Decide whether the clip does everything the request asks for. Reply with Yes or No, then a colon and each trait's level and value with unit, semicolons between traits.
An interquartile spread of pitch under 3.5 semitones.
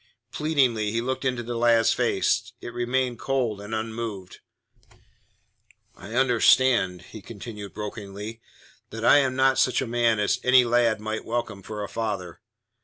Yes: average, 2.9 semitones